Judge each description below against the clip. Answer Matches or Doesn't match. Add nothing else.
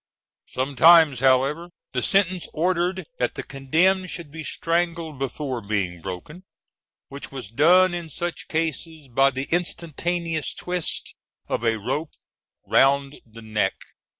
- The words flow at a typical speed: Doesn't match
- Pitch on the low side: Doesn't match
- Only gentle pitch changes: Doesn't match